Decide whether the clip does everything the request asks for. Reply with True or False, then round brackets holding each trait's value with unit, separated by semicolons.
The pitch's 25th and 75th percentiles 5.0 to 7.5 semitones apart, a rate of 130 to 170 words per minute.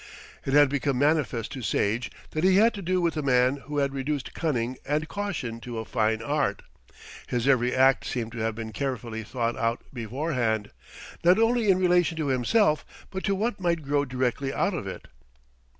False (5.4 semitones; 190 wpm)